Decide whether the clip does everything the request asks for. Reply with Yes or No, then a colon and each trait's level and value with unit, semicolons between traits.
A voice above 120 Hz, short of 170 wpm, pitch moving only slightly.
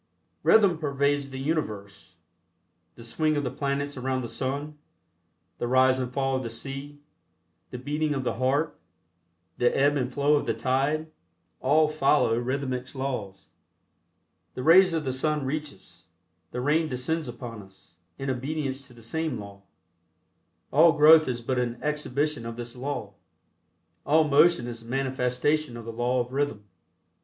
No: low, 135 Hz; average, 160 wpm; average, 3.3 semitones